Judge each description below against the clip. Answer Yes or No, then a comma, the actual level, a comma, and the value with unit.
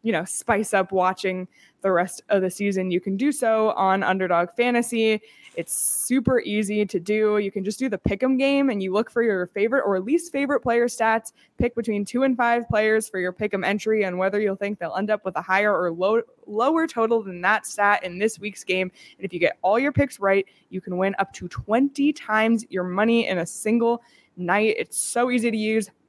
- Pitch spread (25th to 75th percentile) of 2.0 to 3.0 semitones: No, average, 3.5 semitones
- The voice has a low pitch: No, high, 210 Hz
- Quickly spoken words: Yes, fast, 230 wpm